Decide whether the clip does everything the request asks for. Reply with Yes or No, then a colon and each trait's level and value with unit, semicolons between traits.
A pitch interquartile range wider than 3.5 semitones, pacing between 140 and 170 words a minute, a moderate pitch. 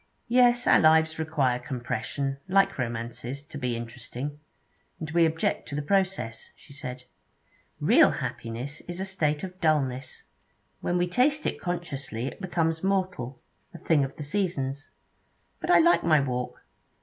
Yes: wide, 5.6 semitones; average, 150 wpm; medium, 150 Hz